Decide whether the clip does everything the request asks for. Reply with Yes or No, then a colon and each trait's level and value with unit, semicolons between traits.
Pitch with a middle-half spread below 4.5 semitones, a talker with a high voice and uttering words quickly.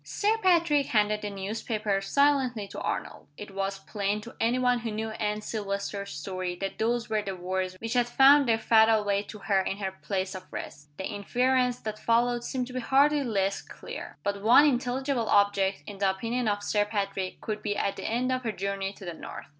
Yes: average, 3.6 semitones; high, 210 Hz; fast, 210 wpm